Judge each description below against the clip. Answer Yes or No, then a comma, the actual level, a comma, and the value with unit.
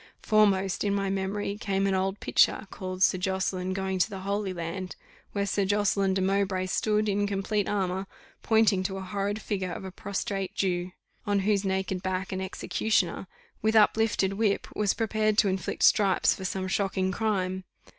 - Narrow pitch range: Yes, narrow, 1.4 semitones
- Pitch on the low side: No, high, 195 Hz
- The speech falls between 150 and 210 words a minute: Yes, average, 175 wpm